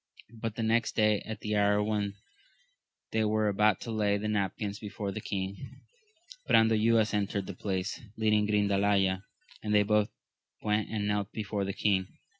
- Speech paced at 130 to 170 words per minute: Yes, average, 160 wpm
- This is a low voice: Yes, low, 105 Hz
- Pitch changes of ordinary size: No, narrow, 1.3 semitones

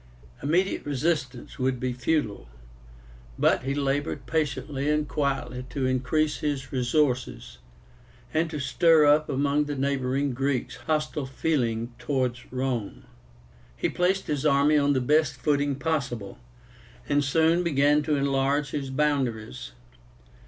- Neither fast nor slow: No, slow, 125 wpm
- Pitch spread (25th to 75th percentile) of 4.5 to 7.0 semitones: No, average, 2.8 semitones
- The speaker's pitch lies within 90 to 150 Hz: Yes, medium, 140 Hz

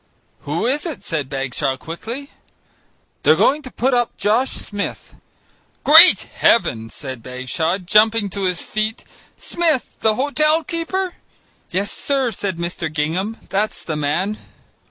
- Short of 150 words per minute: Yes, slow, 135 wpm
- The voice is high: Yes, high, 210 Hz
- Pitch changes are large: Yes, wide, 8.7 semitones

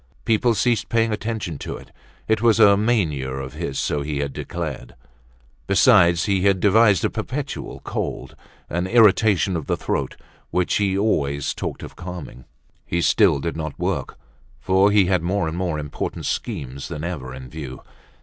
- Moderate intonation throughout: No, wide, 5.8 semitones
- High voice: No, very low, 90 Hz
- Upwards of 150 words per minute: Yes, average, 170 wpm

